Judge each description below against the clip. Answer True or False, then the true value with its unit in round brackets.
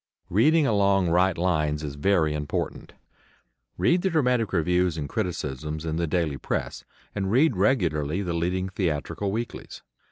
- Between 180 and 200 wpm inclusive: False (140 wpm)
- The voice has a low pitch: True (90 Hz)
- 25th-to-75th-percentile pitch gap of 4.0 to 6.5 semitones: True (4.7 semitones)